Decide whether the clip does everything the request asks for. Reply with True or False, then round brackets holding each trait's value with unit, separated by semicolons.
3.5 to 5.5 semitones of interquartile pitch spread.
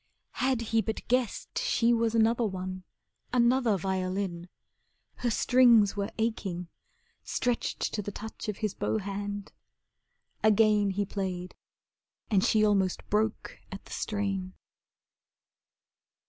False (2.9 semitones)